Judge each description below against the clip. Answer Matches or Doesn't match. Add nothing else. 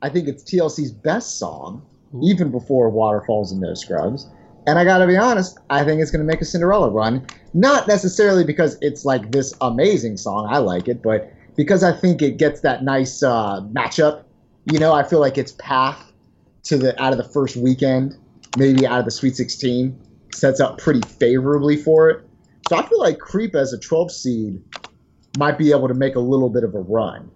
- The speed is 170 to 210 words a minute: Matches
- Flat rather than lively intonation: Doesn't match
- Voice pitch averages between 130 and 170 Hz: Matches